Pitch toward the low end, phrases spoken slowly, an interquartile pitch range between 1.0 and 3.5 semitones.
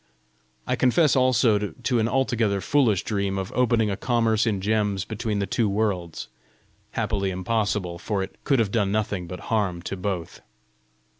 No: low, 105 Hz; average, 160 wpm; average, 3.0 semitones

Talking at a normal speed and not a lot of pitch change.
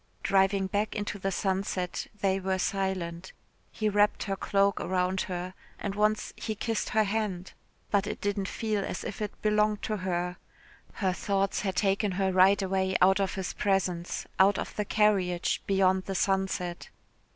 Yes: average, 165 wpm; narrow, 1.5 semitones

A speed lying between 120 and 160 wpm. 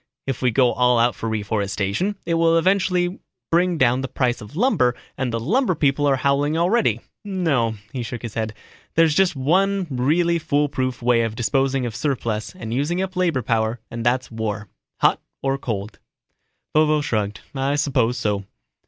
No: average, 170 wpm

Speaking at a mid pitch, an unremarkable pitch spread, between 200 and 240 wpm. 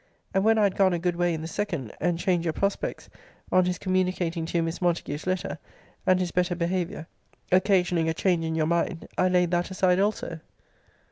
No: medium, 175 Hz; narrow, 1.8 semitones; fast, 205 wpm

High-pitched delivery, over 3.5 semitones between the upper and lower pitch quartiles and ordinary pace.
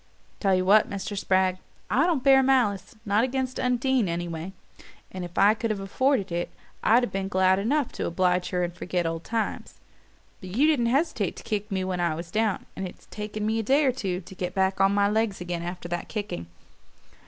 No: high, 200 Hz; average, 4.1 semitones; fast, 210 wpm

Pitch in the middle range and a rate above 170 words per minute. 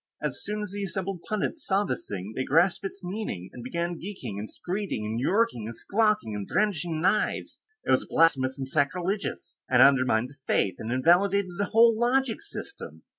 Yes: medium, 175 Hz; average, 180 wpm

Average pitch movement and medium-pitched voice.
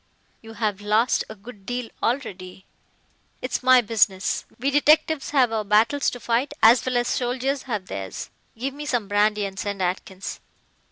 No: average, 3.9 semitones; high, 225 Hz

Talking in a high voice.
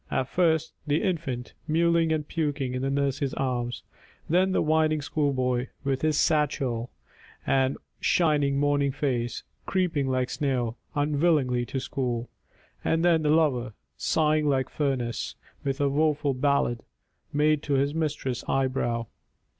No: medium, 140 Hz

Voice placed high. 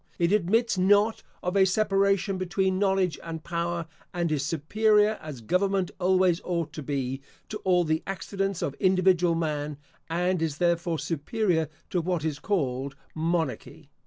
No: medium, 175 Hz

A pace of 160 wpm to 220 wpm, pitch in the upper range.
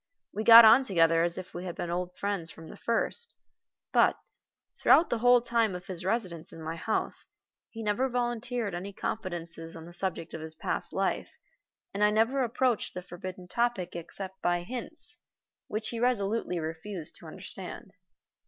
Yes: average, 170 wpm; high, 195 Hz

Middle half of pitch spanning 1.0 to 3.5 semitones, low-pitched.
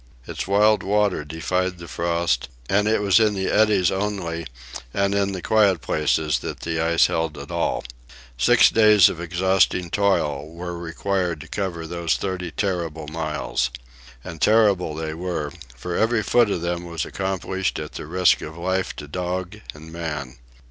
Yes: average, 3.1 semitones; very low, 90 Hz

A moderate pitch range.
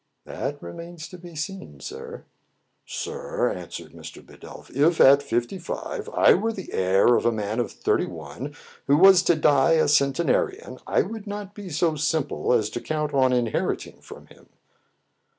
No: wide, 7.3 semitones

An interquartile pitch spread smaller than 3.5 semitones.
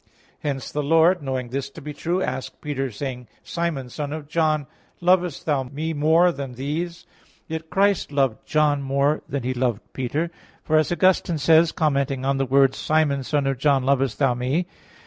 Yes: average, 3.1 semitones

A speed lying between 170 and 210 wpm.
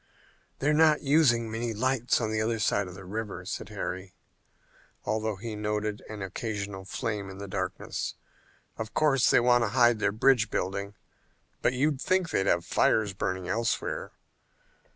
No: average, 160 wpm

